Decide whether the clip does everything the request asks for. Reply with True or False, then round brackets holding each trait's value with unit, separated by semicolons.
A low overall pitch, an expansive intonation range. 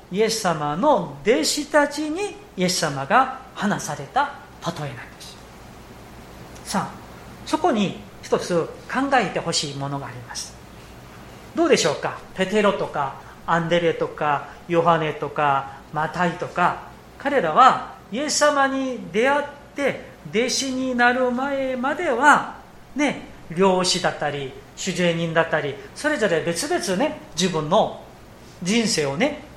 False (195 Hz; 8.6 semitones)